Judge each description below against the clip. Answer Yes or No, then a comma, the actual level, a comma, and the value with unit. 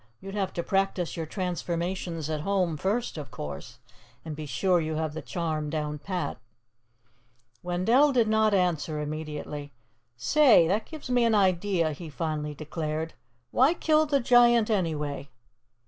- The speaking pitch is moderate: Yes, medium, 170 Hz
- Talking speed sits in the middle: Yes, average, 145 wpm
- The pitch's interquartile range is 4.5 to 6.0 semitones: Yes, average, 5.1 semitones